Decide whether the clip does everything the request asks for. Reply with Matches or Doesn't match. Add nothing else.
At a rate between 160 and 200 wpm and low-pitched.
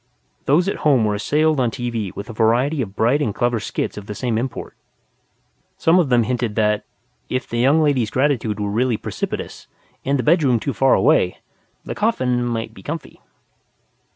Matches